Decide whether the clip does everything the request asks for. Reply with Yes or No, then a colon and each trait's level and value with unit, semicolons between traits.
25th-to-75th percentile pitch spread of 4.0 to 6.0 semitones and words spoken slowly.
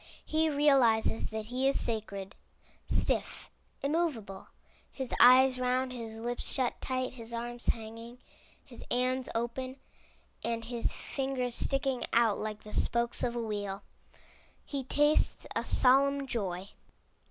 No: average, 2.7 semitones; slow, 130 wpm